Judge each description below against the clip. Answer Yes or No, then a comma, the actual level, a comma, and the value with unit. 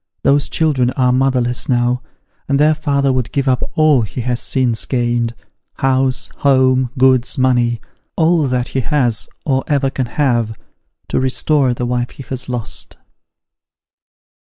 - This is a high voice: No, low, 130 Hz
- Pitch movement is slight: Yes, narrow, 2.0 semitones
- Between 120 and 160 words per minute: Yes, average, 145 wpm